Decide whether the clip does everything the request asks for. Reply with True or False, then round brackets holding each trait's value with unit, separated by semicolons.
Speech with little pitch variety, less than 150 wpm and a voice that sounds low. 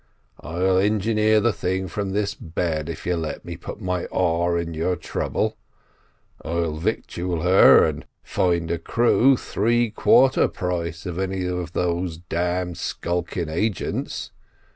True (2.3 semitones; 140 wpm; 90 Hz)